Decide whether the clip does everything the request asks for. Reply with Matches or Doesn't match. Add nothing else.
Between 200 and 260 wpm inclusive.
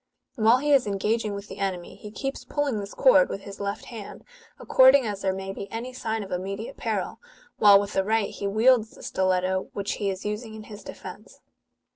Matches